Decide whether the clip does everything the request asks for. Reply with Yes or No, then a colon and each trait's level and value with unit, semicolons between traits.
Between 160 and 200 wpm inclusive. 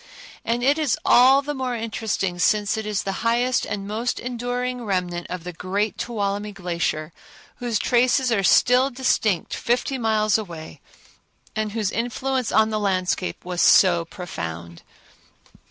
No: average, 145 wpm